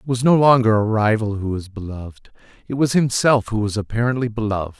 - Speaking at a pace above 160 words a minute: Yes, average, 200 wpm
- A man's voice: Yes, male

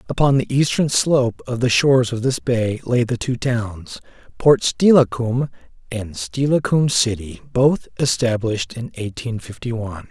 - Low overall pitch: Yes, low, 120 Hz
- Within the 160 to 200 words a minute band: No, average, 150 wpm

